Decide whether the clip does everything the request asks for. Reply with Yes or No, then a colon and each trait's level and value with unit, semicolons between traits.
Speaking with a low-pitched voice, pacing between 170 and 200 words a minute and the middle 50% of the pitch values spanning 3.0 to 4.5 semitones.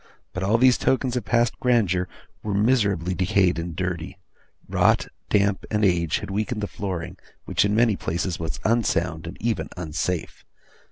No: low, 100 Hz; average, 160 wpm; average, 4.1 semitones